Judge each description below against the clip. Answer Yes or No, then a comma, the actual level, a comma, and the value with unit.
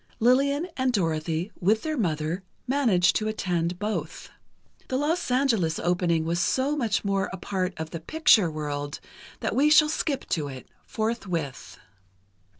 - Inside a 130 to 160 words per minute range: Yes, average, 150 wpm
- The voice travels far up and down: Yes, wide, 7.7 semitones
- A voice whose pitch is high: Yes, high, 195 Hz